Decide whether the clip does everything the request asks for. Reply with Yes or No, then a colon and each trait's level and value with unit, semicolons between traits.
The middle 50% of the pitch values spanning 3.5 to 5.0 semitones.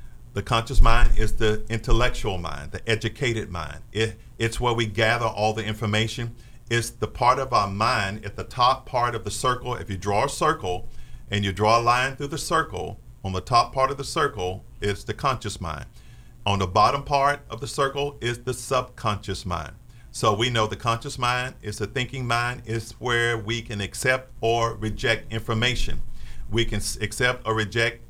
No: average, 2.7 semitones